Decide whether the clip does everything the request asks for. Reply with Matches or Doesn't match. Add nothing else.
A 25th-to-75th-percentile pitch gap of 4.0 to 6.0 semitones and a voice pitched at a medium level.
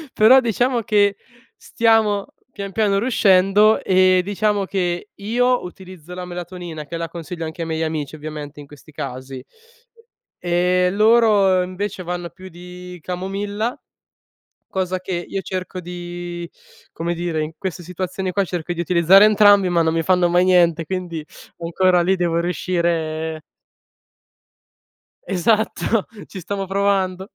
Doesn't match